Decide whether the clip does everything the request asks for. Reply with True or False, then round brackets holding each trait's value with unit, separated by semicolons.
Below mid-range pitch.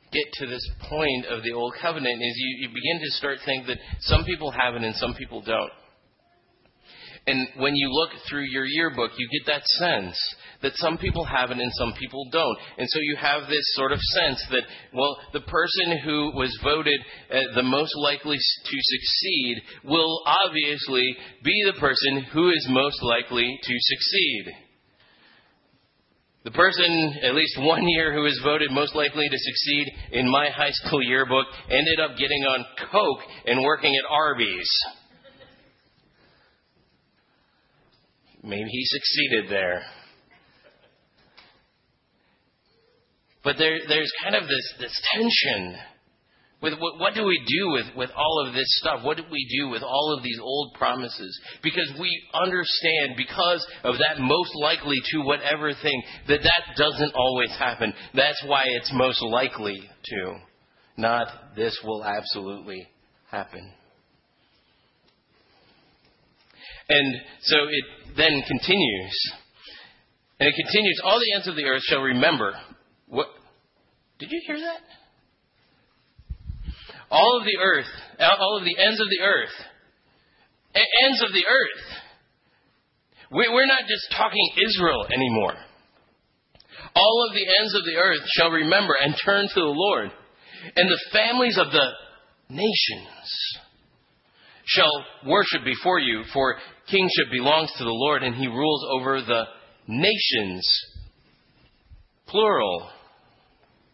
False (145 Hz)